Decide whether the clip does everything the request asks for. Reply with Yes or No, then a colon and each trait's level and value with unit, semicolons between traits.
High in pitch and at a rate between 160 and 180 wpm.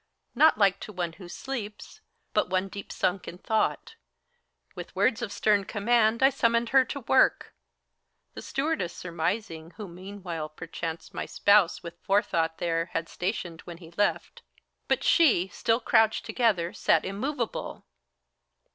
No: high, 200 Hz; average, 145 wpm